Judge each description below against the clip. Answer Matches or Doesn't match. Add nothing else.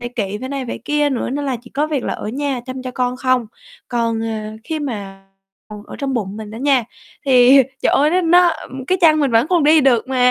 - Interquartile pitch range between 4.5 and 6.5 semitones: Doesn't match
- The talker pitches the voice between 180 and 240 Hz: Doesn't match